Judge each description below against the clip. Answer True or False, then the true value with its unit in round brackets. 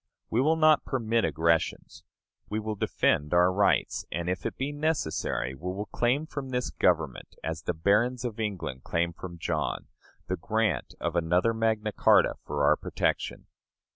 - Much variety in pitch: True (6.3 semitones)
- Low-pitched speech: True (105 Hz)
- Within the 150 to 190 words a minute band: True (165 wpm)